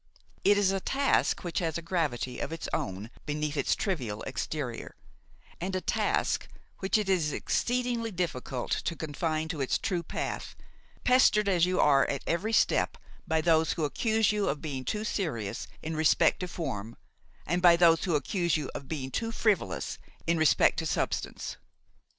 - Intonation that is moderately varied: Yes, average, 4.9 semitones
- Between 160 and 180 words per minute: Yes, average, 170 wpm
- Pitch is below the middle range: No, medium, 165 Hz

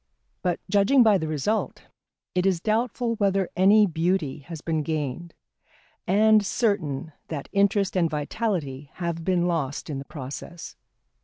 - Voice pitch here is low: No, medium, 175 Hz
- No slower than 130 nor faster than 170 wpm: Yes, average, 140 wpm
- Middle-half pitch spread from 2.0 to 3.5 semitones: No, average, 4.5 semitones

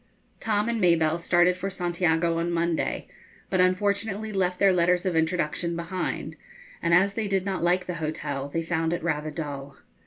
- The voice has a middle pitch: Yes, medium, 175 Hz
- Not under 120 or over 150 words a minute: No, average, 175 wpm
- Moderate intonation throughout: No, narrow, 2.3 semitones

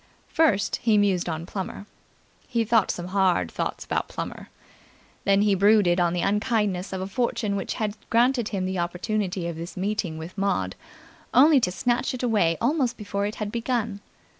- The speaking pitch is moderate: No, high, 200 Hz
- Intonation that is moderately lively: Yes, average, 4.0 semitones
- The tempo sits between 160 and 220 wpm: Yes, average, 175 wpm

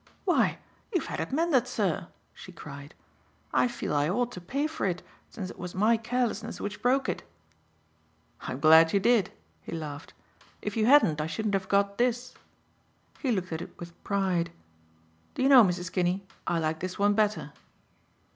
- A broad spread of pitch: Yes, wide, 5.9 semitones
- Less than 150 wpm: No, average, 175 wpm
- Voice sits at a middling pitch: No, high, 200 Hz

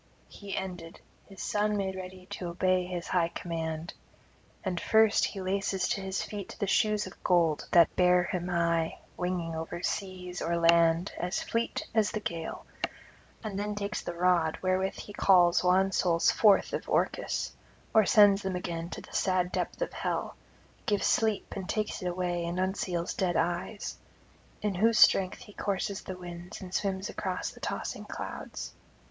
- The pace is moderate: Yes, average, 165 wpm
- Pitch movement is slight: Yes, narrow, 2.3 semitones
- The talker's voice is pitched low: No, medium, 185 Hz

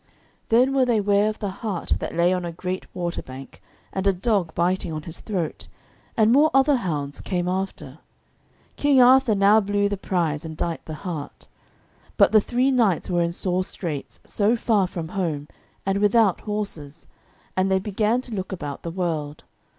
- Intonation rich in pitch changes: No, average, 4.1 semitones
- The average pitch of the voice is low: No, high, 190 Hz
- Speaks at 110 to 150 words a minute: No, average, 180 wpm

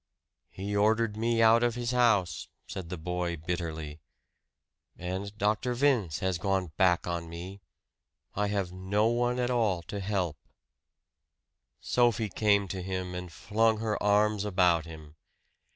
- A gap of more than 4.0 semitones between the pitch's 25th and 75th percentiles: No, average, 3.7 semitones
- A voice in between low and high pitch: No, low, 100 Hz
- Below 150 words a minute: Yes, average, 140 wpm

